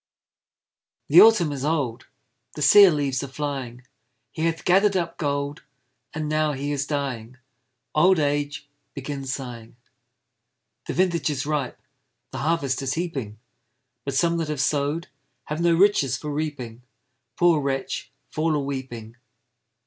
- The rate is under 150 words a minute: Yes, average, 140 wpm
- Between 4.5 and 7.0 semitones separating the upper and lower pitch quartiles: No, average, 3.2 semitones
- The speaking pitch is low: No, medium, 145 Hz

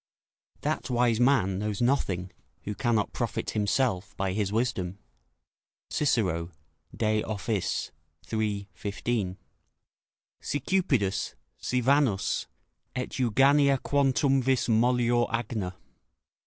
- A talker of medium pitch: No, low, 115 Hz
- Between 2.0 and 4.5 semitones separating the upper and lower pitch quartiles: Yes, average, 4.2 semitones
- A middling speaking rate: No, slow, 95 wpm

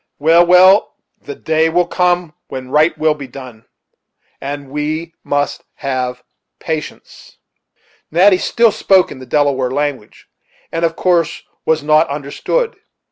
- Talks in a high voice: No, medium, 155 Hz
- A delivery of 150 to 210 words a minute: No, slow, 135 wpm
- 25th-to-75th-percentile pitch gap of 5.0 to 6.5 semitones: No, average, 3.8 semitones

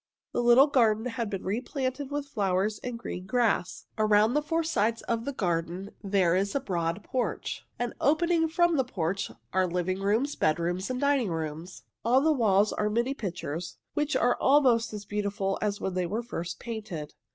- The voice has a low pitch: No, high, 215 Hz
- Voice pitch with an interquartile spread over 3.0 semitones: Yes, wide, 5.6 semitones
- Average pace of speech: Yes, average, 180 wpm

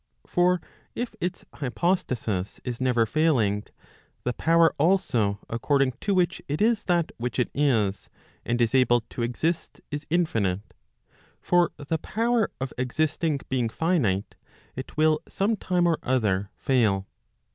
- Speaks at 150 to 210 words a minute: No, slow, 135 wpm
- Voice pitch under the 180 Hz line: Yes, medium, 140 Hz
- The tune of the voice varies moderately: No, wide, 6.5 semitones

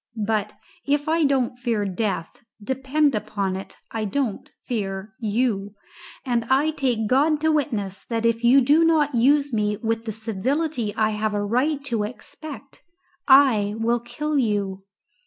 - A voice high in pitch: Yes, high, 235 Hz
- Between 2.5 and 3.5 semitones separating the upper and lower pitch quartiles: No, average, 4.9 semitones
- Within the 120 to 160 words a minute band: Yes, average, 155 wpm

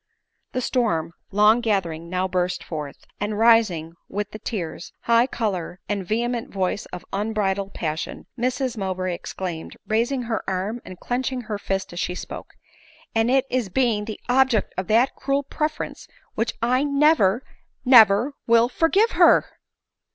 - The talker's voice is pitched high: Yes, high, 215 Hz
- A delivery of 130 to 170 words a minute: Yes, average, 150 wpm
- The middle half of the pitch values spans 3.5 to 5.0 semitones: Yes, average, 4.7 semitones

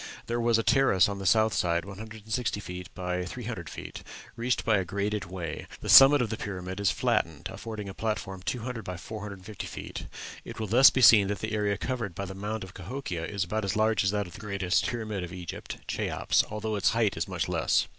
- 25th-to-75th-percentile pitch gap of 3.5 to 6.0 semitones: No, average, 3.0 semitones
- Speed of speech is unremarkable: No, fast, 215 wpm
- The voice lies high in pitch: No, low, 105 Hz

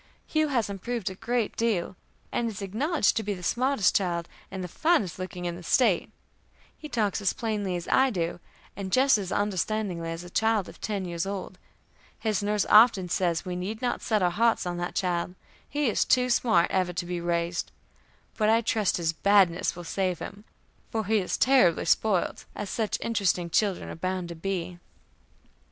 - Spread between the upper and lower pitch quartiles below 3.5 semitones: No, average, 3.9 semitones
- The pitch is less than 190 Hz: No, high, 195 Hz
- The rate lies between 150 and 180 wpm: No, average, 190 wpm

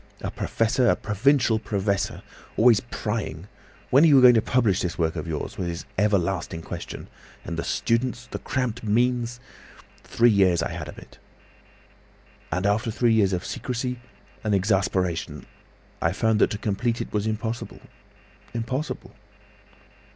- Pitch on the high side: No, low, 110 Hz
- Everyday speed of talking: Yes, average, 145 wpm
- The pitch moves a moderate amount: Yes, average, 4.3 semitones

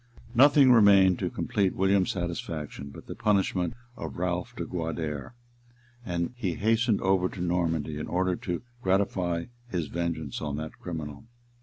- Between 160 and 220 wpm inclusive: No, average, 145 wpm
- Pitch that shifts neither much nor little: Yes, average, 3.1 semitones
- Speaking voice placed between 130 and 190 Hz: No, very low, 90 Hz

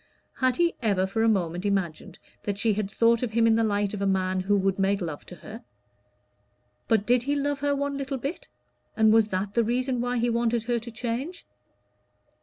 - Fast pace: Yes, fast, 210 wpm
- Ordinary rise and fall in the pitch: Yes, average, 3.8 semitones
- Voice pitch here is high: Yes, high, 225 Hz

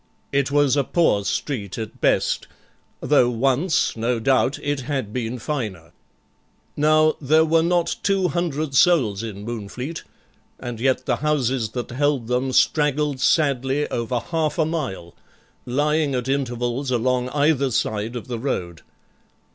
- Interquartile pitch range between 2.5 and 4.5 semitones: Yes, average, 3.9 semitones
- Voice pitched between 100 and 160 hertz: Yes, low, 135 Hz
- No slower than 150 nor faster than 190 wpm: No, average, 140 wpm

